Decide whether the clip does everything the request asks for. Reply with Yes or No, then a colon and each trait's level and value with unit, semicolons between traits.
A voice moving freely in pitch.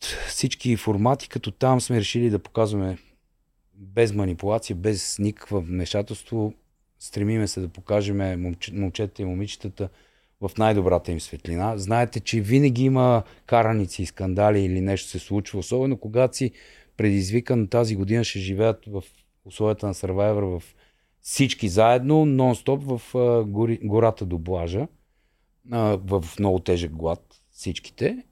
No: average, 3.3 semitones